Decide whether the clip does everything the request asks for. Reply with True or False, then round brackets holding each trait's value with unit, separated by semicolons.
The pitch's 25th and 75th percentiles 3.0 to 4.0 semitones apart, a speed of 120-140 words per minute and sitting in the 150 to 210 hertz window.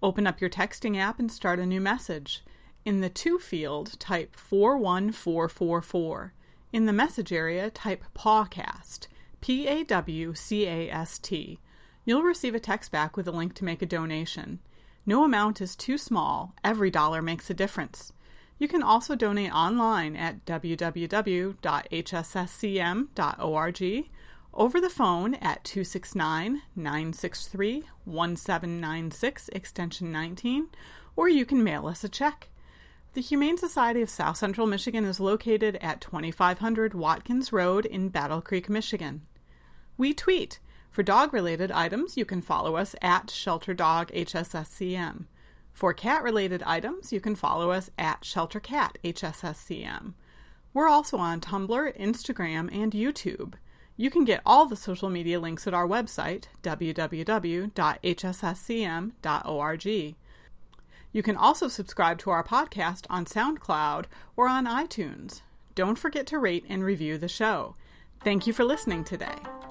False (4.9 semitones; 135 wpm; 190 Hz)